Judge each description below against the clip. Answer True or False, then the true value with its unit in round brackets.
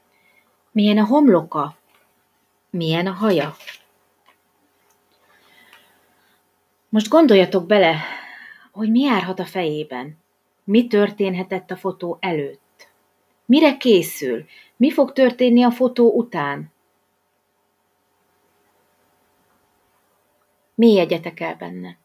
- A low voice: False (195 Hz)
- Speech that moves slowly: True (85 wpm)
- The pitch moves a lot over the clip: True (5.8 semitones)